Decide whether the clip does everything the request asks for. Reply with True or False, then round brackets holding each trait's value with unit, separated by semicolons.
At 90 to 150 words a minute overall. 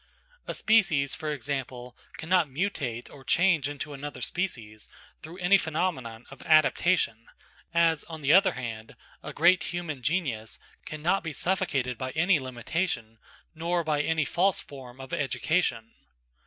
True (140 wpm)